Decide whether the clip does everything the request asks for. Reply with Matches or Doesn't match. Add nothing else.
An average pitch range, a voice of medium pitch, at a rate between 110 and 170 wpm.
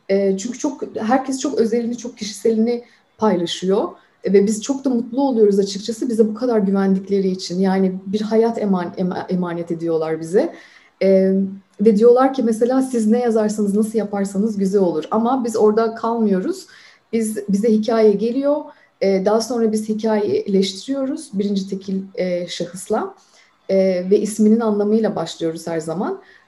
Doesn't match